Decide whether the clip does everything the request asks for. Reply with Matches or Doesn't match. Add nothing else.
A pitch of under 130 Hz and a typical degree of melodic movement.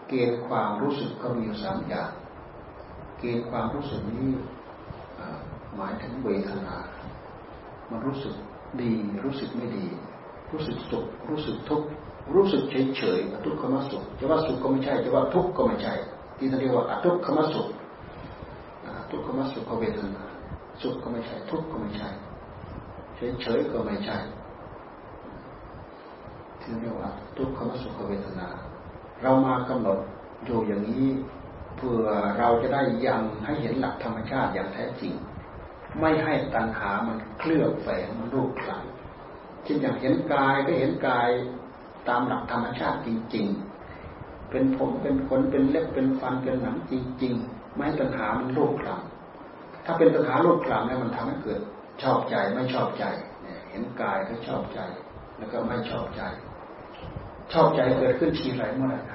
Matches